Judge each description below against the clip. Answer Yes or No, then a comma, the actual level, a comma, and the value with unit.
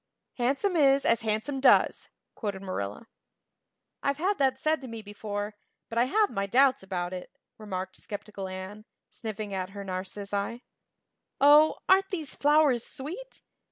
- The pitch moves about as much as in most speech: No, wide, 6.0 semitones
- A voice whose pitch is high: Yes, high, 225 Hz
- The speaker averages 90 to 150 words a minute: Yes, average, 145 wpm